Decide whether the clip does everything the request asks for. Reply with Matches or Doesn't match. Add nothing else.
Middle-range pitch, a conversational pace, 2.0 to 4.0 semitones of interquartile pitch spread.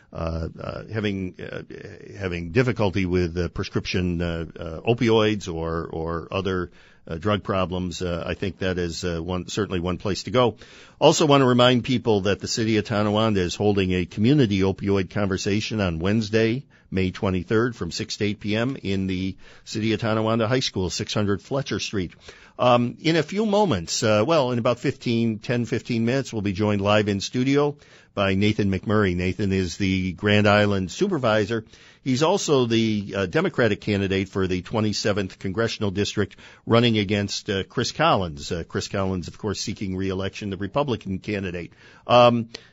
Doesn't match